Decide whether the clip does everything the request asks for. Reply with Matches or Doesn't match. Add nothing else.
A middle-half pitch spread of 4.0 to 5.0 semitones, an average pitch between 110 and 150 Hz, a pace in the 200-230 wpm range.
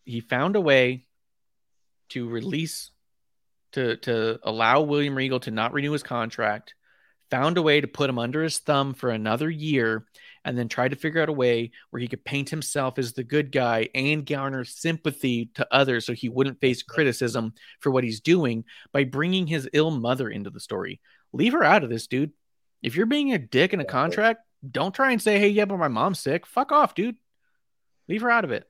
Matches